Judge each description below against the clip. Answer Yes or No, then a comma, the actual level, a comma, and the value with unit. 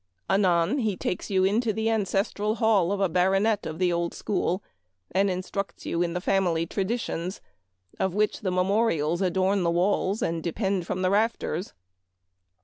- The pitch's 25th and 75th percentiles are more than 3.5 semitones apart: No, average, 2.7 semitones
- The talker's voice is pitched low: No, high, 190 Hz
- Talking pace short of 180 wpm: Yes, average, 170 wpm